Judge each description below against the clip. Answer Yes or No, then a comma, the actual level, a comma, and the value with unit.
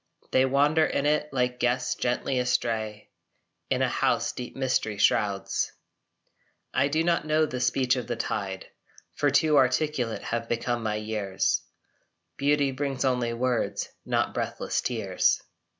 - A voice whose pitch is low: Yes, low, 125 Hz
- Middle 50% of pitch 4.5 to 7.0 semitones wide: No, average, 3.3 semitones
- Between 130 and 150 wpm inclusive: Yes, average, 140 wpm